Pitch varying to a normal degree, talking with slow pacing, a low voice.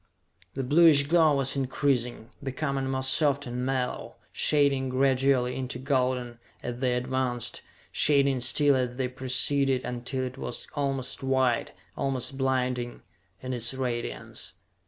No: narrow, 1.7 semitones; slow, 130 wpm; low, 130 Hz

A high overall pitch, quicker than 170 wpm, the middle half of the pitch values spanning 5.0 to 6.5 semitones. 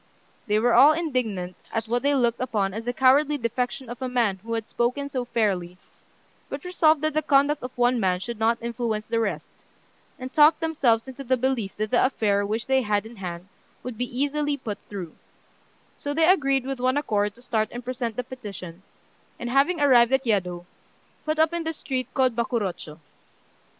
No: high, 245 Hz; average, 195 wpm; average, 4.2 semitones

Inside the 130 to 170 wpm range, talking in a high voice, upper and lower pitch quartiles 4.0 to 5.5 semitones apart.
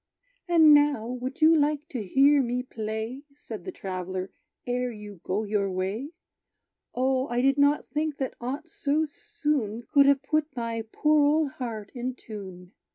Yes: average, 160 wpm; very high, 255 Hz; average, 5.2 semitones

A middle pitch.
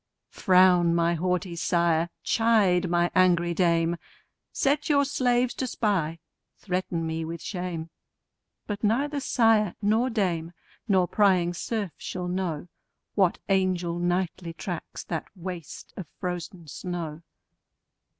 Yes: medium, 180 Hz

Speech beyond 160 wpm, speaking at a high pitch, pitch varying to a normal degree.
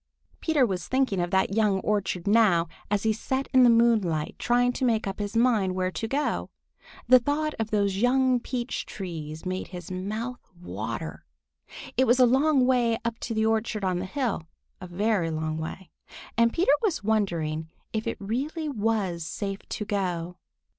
Yes: average, 175 wpm; high, 215 Hz; average, 4.9 semitones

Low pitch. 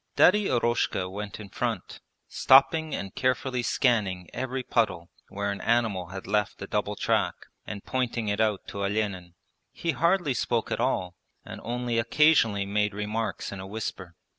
Yes: low, 110 Hz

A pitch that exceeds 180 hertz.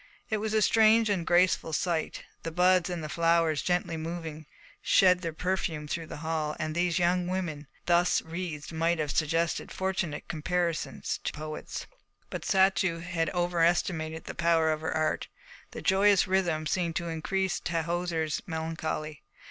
No: medium, 170 Hz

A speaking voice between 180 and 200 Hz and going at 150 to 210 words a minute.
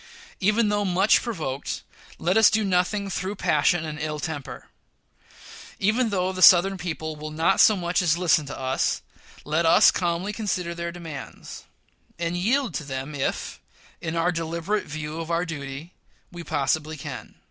No: medium, 170 Hz; average, 160 wpm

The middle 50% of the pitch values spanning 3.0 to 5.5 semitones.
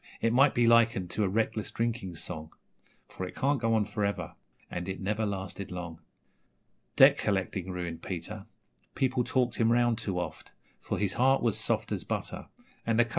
Yes: average, 4.0 semitones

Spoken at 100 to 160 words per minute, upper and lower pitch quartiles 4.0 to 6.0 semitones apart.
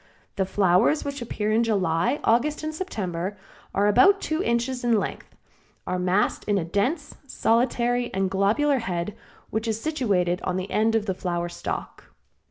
No: average, 170 wpm; average, 4.8 semitones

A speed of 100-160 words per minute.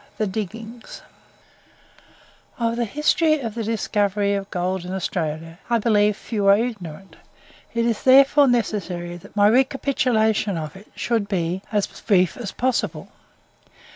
Yes: average, 140 wpm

